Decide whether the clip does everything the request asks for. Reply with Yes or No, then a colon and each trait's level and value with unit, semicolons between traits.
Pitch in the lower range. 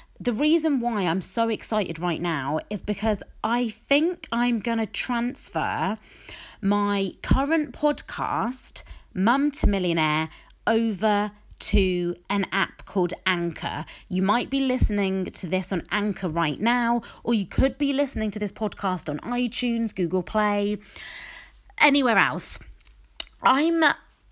No: high, 210 Hz